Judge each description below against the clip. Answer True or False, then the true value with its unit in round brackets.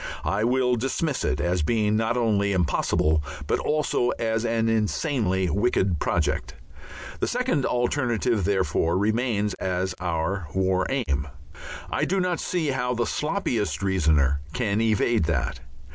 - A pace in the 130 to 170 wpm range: True (135 wpm)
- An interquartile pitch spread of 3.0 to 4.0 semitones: False (4.9 semitones)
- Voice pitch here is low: True (110 Hz)